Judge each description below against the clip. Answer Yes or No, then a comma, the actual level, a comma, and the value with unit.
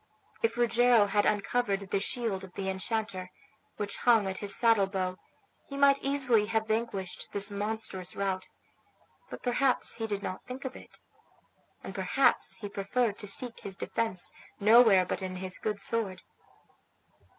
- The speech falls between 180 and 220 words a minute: No, average, 155 wpm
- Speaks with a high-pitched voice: Yes, high, 205 Hz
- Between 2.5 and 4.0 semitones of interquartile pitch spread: Yes, average, 3.3 semitones